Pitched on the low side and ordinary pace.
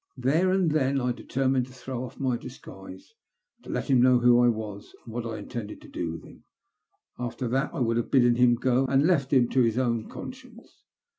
No: low, 125 Hz; fast, 220 wpm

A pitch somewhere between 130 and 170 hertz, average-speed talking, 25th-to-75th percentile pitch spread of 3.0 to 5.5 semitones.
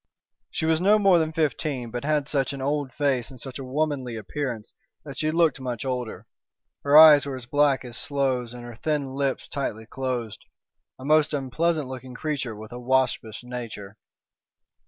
Yes: low, 135 Hz; average, 180 wpm; average, 3.3 semitones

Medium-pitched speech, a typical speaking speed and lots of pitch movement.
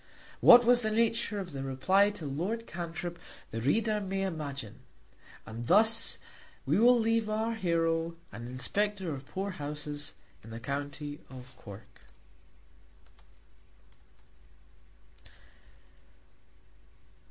No: medium, 170 Hz; slow, 105 wpm; wide, 7.5 semitones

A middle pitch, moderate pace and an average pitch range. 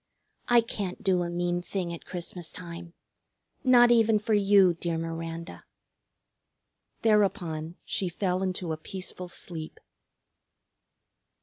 No: medium, 180 Hz; slow, 115 wpm; average, 3.2 semitones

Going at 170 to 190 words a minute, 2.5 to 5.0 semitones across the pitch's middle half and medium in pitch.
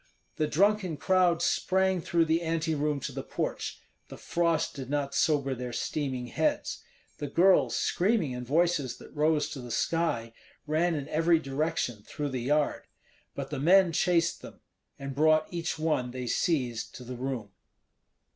No: average, 160 wpm; average, 4.1 semitones; medium, 150 Hz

